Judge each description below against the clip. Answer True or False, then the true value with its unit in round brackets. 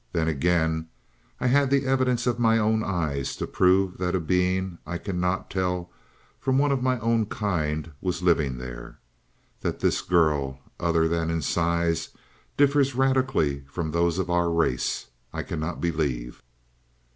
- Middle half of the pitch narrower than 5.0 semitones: False (5.5 semitones)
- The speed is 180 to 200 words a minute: False (155 wpm)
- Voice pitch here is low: True (90 Hz)